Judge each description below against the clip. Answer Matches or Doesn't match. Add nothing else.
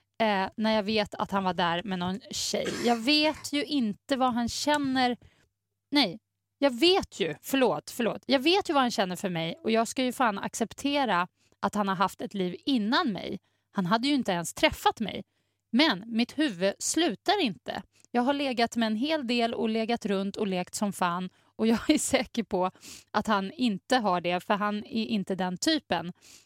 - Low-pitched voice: Doesn't match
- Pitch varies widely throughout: Matches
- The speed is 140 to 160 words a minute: Doesn't match